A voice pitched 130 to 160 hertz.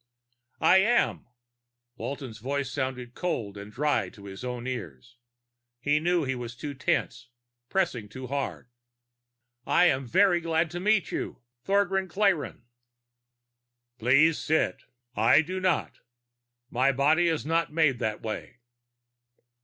Yes: medium, 140 Hz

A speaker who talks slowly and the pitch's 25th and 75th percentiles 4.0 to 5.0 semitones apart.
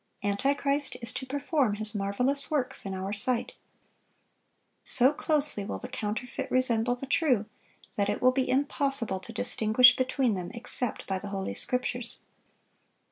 No: average, 145 wpm; average, 4.6 semitones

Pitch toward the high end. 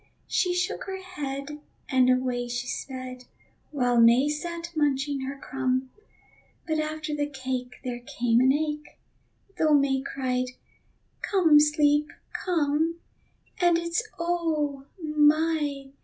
Yes: very high, 290 Hz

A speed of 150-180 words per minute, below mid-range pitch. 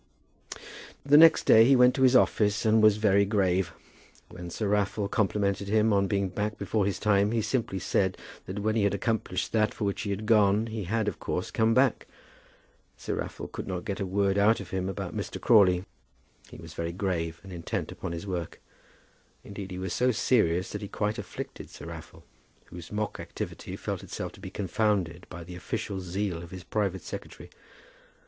No: average, 195 wpm; low, 100 Hz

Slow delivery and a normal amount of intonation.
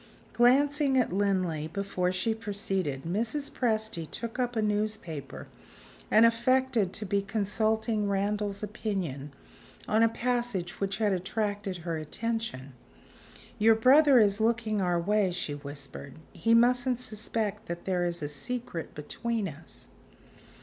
Yes: slow, 130 wpm; average, 4.2 semitones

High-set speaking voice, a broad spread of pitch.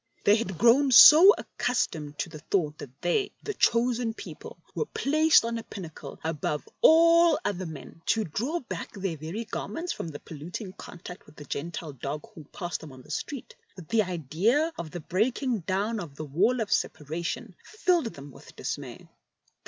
Yes: high, 195 Hz; wide, 7.4 semitones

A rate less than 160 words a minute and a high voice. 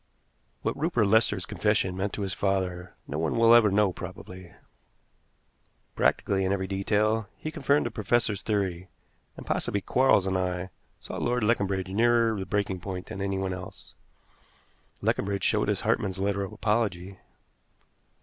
No: average, 150 wpm; low, 100 Hz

